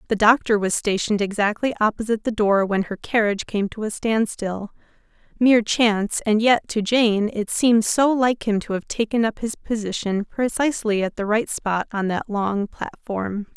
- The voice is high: Yes, high, 215 Hz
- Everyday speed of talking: Yes, average, 180 wpm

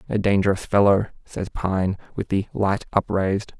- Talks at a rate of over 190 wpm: No, average, 150 wpm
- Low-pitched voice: Yes, low, 100 Hz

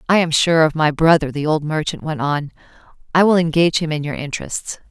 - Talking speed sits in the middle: No, fast, 220 wpm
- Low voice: No, medium, 155 Hz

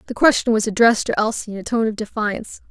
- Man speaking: No, female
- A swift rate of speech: Yes, fast, 245 wpm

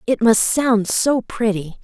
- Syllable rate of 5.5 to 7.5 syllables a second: No, 3.7 syllables/s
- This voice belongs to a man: No, female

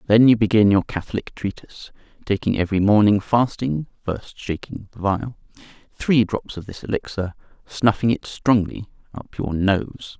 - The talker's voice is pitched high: No, low, 105 Hz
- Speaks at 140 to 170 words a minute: Yes, average, 145 wpm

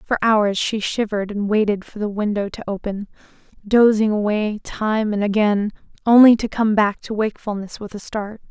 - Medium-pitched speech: No, high, 210 Hz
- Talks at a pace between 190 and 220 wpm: No, average, 175 wpm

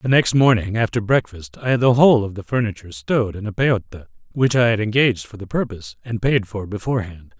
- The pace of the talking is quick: Yes, fast, 220 wpm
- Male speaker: Yes, male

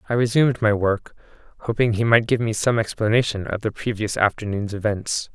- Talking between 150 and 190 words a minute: Yes, average, 180 wpm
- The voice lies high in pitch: No, low, 110 Hz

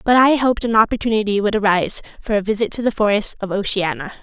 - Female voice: Yes, female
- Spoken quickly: Yes, fast, 215 wpm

